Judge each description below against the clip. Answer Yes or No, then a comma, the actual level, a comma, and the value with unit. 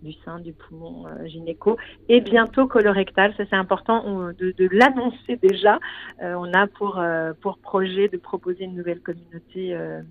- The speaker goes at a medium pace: Yes, average, 170 wpm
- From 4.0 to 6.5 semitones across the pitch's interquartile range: No, average, 3.2 semitones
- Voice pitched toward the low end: No, high, 190 Hz